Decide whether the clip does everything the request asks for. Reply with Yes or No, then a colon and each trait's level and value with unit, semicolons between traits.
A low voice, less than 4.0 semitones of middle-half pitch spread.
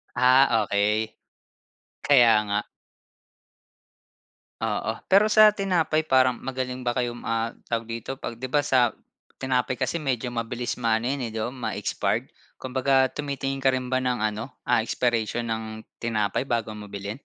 Yes: low, 125 Hz; average, 2.8 semitones